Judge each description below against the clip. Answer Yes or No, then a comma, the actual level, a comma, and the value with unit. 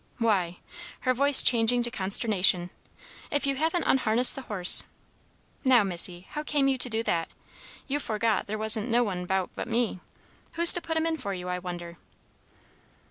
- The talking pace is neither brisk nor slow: Yes, average, 175 wpm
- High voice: Yes, high, 225 Hz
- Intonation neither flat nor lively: No, wide, 6.2 semitones